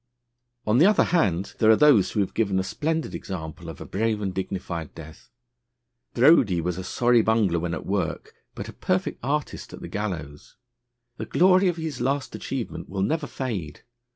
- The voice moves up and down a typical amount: No, wide, 7.2 semitones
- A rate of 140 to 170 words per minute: No, average, 180 wpm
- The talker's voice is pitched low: Yes, low, 105 Hz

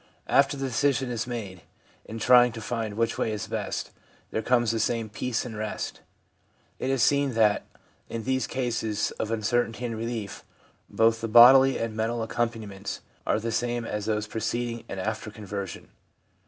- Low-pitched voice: Yes, low, 115 Hz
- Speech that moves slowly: No, average, 170 wpm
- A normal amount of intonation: No, narrow, 1.9 semitones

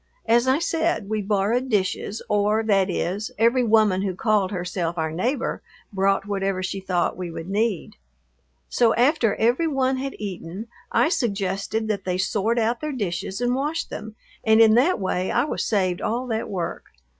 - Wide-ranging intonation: No, average, 3.9 semitones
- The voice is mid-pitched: No, high, 210 Hz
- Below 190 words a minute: Yes, average, 175 wpm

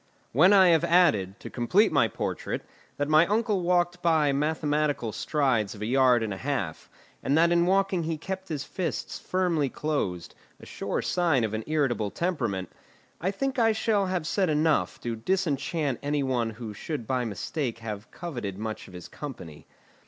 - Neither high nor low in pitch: Yes, medium, 150 Hz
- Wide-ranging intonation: Yes, wide, 7.1 semitones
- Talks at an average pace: Yes, average, 175 wpm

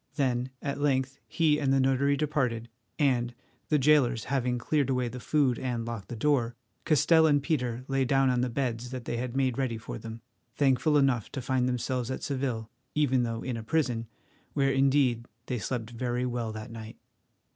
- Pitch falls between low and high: No, low, 130 Hz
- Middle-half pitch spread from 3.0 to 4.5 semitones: No, narrow, 2.5 semitones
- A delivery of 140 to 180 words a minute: No, average, 190 wpm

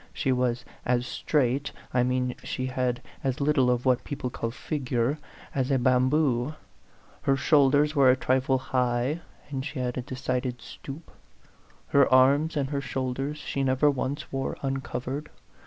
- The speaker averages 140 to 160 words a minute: Yes, average, 155 wpm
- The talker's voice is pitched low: Yes, low, 130 Hz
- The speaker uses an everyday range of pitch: No, narrow, 1.9 semitones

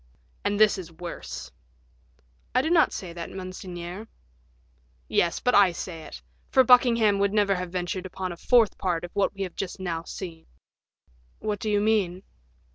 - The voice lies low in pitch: No, high, 190 Hz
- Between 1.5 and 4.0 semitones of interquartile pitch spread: Yes, average, 3.1 semitones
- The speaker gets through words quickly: No, average, 170 wpm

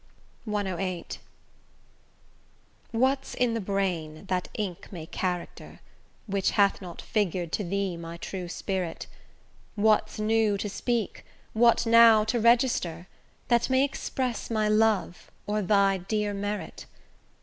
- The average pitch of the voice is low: No, high, 205 Hz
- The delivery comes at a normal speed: No, slow, 120 wpm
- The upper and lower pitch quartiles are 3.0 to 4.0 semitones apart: Yes, average, 3.4 semitones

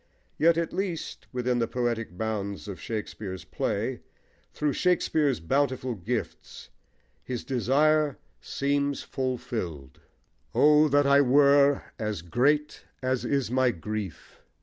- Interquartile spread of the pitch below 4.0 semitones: No, average, 4.6 semitones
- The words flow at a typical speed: No, slow, 115 wpm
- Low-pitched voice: Yes, low, 130 Hz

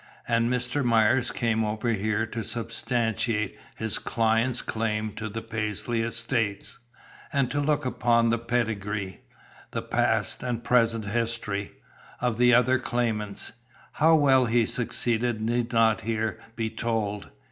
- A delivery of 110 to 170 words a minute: Yes, slow, 135 wpm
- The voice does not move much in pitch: Yes, narrow, 1.9 semitones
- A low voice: Yes, low, 115 Hz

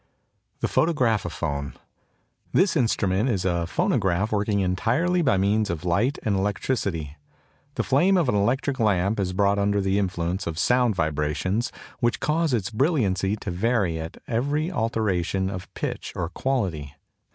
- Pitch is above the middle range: No, low, 100 Hz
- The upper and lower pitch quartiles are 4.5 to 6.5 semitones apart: Yes, average, 5.2 semitones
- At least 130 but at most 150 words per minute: Yes, average, 145 wpm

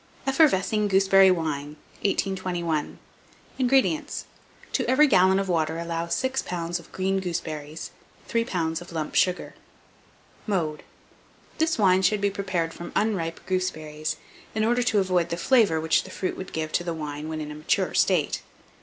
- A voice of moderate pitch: Yes, medium, 180 Hz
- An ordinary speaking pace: Yes, average, 155 wpm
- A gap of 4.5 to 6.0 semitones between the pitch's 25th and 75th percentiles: No, average, 3.7 semitones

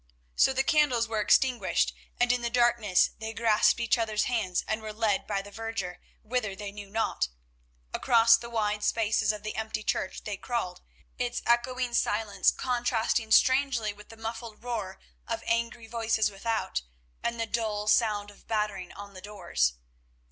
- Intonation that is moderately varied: No, narrow, 2.1 semitones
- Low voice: No, high, 225 Hz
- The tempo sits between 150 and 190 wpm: Yes, average, 165 wpm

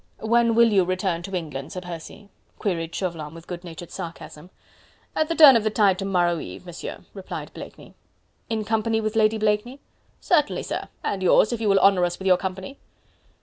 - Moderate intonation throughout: Yes, average, 4.0 semitones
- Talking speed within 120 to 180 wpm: No, average, 190 wpm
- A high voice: Yes, high, 195 Hz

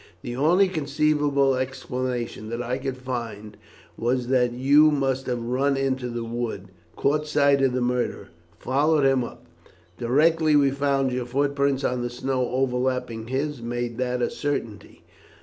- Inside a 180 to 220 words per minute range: No, average, 160 wpm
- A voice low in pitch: Yes, low, 130 Hz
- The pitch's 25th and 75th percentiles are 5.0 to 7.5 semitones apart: No, narrow, 2.5 semitones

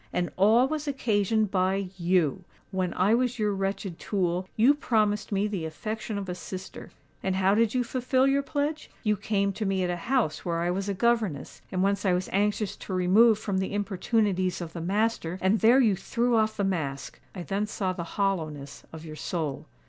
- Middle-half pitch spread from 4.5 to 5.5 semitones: No, average, 3.3 semitones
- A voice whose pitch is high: Yes, high, 195 Hz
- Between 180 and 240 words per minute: Yes, average, 200 wpm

